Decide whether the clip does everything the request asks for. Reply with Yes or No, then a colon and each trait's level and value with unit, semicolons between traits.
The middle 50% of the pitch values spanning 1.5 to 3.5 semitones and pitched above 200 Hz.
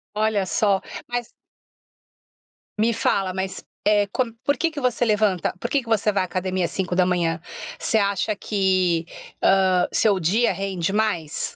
No: average, 2.9 semitones; high, 195 Hz